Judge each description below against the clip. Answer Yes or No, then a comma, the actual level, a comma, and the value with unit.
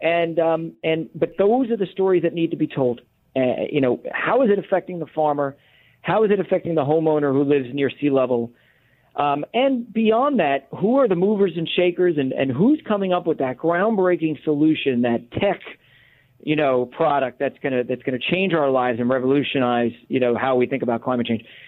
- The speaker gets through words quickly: Yes, fast, 210 wpm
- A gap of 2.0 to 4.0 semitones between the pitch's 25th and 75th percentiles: No, wide, 5.5 semitones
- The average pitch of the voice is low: No, medium, 150 Hz